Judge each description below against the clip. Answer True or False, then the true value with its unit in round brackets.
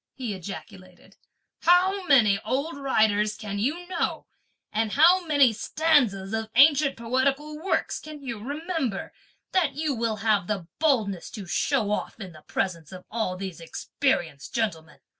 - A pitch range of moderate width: False (6.7 semitones)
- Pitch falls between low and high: False (230 Hz)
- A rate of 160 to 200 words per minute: False (145 wpm)